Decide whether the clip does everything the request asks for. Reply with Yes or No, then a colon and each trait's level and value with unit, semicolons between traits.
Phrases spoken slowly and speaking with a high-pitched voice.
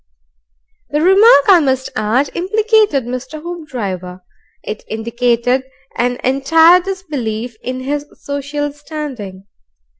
Yes: slow, 100 wpm; very high, 275 Hz